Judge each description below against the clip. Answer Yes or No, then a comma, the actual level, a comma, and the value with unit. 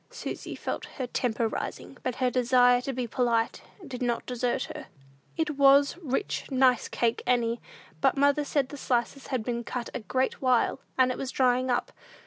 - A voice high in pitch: Yes, very high, 255 Hz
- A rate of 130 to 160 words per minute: No, average, 180 wpm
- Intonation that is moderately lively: No, narrow, 1.8 semitones